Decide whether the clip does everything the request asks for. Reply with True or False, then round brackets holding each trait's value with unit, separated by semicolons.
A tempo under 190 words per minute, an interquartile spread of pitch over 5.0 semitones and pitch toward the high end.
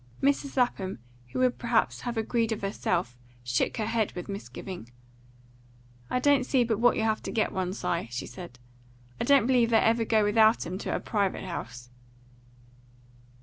False (180 wpm; 4.2 semitones; 220 Hz)